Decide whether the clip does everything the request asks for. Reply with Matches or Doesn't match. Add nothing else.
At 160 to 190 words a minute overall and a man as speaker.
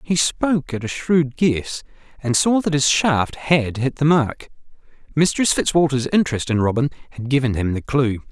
Matches